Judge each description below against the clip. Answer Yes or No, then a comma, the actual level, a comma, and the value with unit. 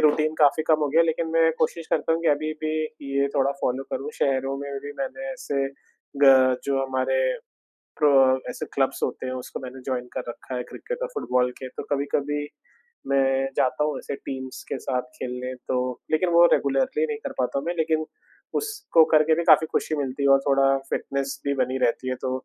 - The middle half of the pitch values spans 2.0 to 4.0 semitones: Yes, average, 3.1 semitones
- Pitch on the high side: No, medium, 140 Hz